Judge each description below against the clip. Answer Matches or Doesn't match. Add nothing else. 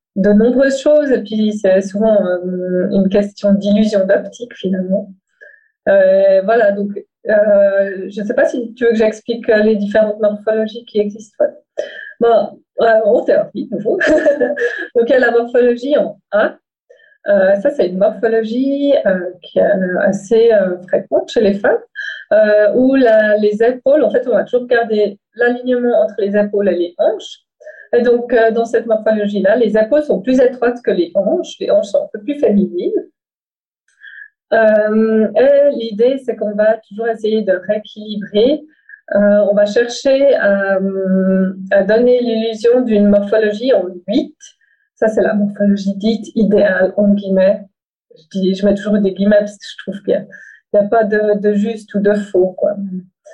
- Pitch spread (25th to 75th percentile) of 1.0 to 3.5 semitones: Doesn't match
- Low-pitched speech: Doesn't match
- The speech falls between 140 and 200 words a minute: Matches